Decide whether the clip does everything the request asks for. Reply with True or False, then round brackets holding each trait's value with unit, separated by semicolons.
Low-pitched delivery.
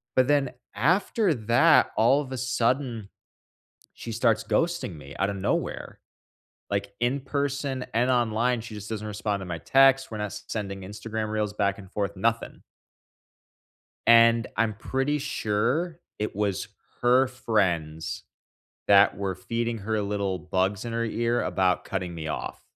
True (110 Hz)